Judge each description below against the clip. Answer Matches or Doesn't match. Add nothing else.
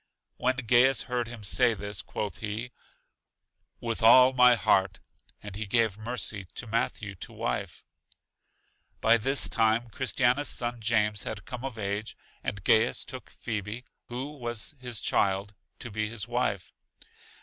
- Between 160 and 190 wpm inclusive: Doesn't match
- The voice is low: Matches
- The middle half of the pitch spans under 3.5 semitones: Matches